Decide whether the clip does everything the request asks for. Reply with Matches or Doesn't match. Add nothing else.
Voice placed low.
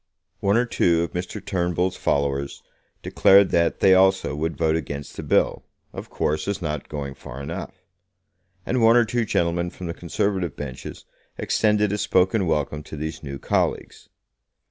Matches